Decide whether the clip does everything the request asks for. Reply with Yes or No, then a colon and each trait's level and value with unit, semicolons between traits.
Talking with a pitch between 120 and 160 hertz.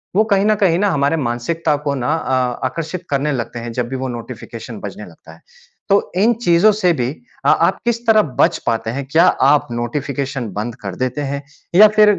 Yes: medium, 140 Hz